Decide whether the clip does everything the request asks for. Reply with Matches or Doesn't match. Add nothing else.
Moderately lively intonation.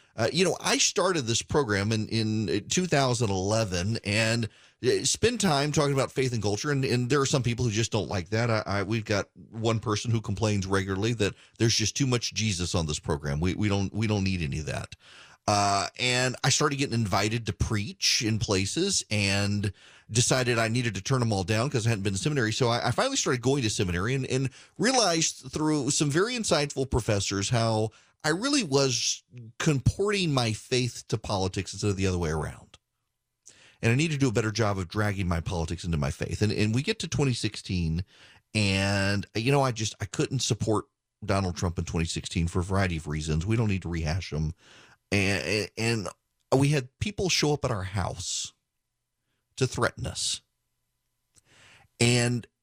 Matches